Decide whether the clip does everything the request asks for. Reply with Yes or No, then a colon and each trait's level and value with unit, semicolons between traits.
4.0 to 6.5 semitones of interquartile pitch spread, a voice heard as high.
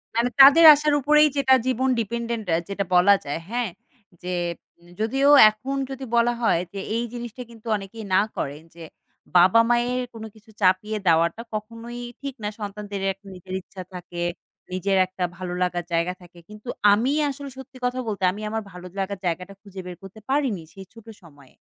Yes: average, 4.6 semitones; high, 215 Hz